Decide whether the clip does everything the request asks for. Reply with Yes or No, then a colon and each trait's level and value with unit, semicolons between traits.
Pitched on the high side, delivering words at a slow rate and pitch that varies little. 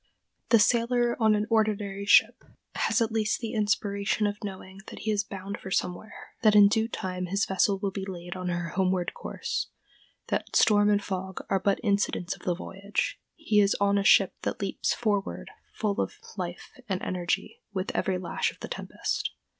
No: high, 200 Hz; average, 185 wpm; narrow, 2.0 semitones